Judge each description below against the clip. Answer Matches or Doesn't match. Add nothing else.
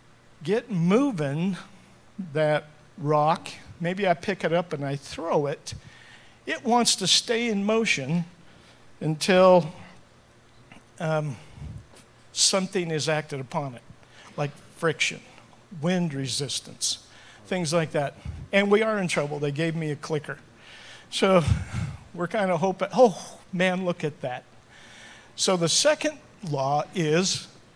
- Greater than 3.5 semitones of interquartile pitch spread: Matches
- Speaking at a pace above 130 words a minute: Doesn't match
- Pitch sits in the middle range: Matches